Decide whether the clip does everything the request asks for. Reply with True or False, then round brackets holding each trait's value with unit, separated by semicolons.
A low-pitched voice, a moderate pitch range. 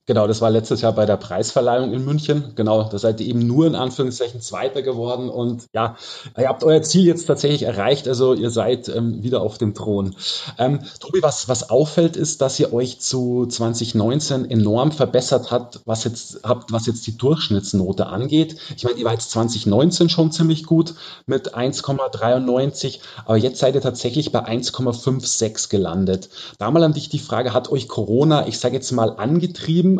True (125 Hz; 4.1 semitones)